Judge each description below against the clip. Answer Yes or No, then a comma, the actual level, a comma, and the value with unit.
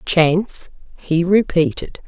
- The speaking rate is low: Yes, slow, 85 wpm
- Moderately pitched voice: Yes, medium, 170 Hz